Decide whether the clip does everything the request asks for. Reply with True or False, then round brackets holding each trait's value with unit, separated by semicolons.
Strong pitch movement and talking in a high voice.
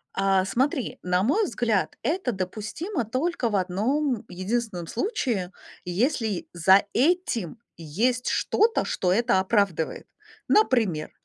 True (5.8 semitones; 220 Hz)